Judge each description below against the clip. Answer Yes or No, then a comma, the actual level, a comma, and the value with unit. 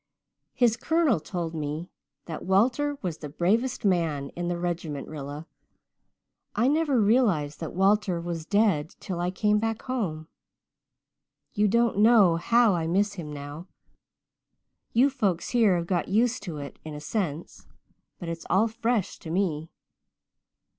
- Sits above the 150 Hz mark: Yes, medium, 185 Hz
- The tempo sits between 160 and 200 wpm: No, average, 145 wpm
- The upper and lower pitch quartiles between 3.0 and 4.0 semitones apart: No, wide, 5.6 semitones